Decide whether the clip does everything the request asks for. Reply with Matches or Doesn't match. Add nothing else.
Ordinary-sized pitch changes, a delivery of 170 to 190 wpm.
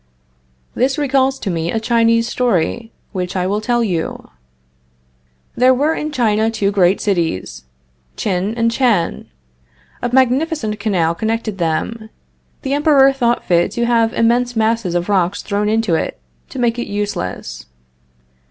Doesn't match